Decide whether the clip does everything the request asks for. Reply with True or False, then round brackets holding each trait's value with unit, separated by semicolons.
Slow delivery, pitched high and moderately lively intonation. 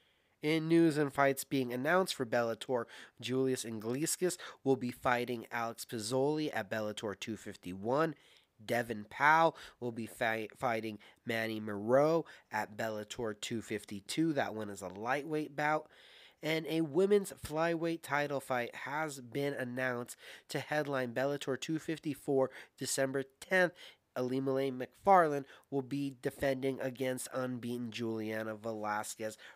False (120 wpm; 130 Hz; 4.5 semitones)